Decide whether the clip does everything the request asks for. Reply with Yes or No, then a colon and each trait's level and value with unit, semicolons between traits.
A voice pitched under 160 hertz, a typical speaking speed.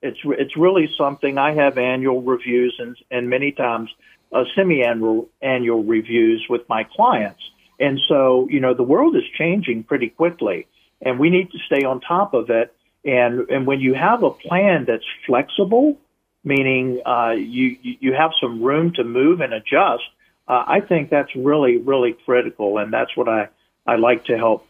Yes: low, 135 Hz; average, 180 wpm